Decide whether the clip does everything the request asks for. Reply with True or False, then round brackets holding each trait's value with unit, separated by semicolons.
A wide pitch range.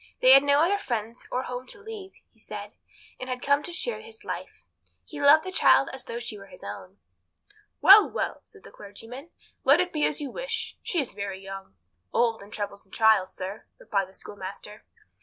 True (8.6 semitones)